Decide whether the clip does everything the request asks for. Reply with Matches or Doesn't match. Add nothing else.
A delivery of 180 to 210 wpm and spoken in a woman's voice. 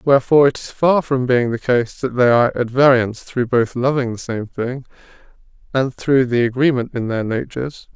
Doesn't match